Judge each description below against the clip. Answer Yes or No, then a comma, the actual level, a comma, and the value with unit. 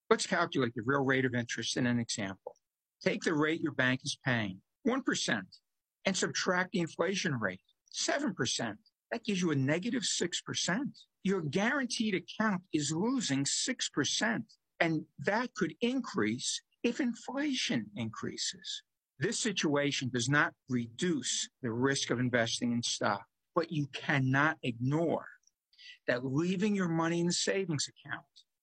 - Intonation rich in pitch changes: Yes, wide, 7.8 semitones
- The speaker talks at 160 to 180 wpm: No, average, 140 wpm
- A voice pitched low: No, medium, 160 Hz